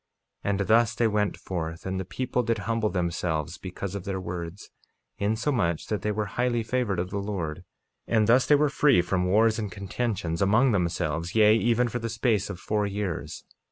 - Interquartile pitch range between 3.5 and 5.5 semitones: Yes, average, 4.0 semitones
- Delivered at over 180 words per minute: Yes, average, 195 wpm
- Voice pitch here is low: Yes, low, 105 Hz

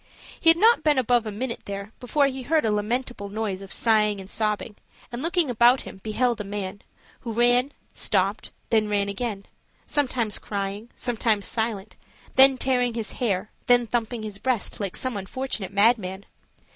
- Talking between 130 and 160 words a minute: No, average, 170 wpm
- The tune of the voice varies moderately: Yes, average, 3.5 semitones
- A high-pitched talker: Yes, high, 225 Hz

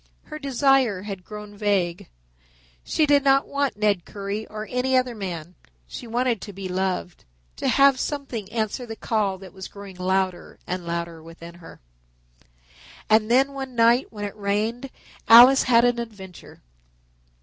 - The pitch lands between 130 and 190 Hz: No, high, 215 Hz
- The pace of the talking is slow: No, average, 155 wpm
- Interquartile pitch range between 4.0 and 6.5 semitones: Yes, average, 4.8 semitones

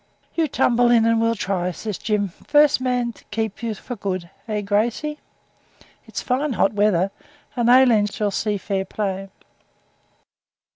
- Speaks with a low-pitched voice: No, high, 220 Hz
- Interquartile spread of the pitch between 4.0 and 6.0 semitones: No, average, 3.5 semitones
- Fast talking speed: No, average, 150 wpm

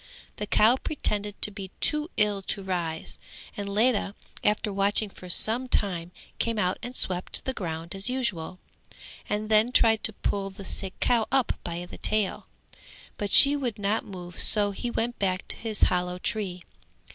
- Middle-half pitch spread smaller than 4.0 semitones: Yes, average, 3.2 semitones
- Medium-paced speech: Yes, average, 170 wpm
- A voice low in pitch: No, high, 205 Hz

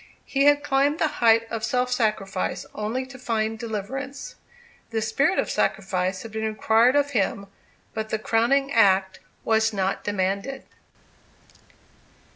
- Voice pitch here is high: Yes, high, 225 Hz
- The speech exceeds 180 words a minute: No, slow, 135 wpm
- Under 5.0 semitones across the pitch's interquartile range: Yes, average, 4.3 semitones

